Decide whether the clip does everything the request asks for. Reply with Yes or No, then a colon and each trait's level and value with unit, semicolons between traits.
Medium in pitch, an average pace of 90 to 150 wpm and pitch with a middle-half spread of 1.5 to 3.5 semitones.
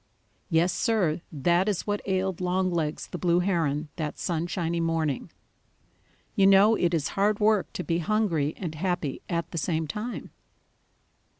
Yes: medium, 175 Hz; average, 145 wpm; average, 3.0 semitones